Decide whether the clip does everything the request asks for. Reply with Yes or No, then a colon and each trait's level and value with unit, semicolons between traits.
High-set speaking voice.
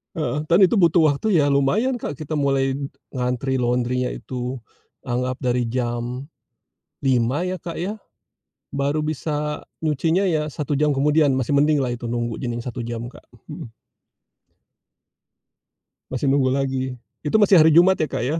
No: medium, 140 Hz